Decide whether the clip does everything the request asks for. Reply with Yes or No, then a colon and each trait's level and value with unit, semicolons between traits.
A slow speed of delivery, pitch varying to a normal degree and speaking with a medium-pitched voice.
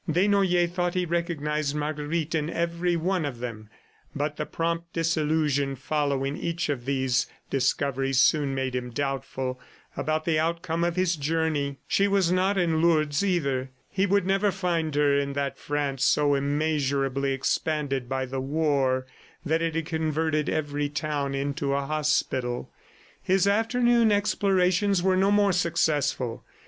No: average, 145 wpm; average, 3.7 semitones; medium, 155 Hz